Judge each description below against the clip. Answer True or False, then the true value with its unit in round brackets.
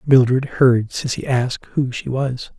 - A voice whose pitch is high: False (130 Hz)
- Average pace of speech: True (165 wpm)